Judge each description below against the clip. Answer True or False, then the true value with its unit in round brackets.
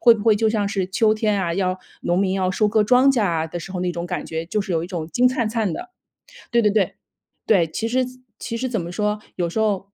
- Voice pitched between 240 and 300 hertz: False (205 Hz)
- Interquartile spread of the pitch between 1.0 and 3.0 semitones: False (3.8 semitones)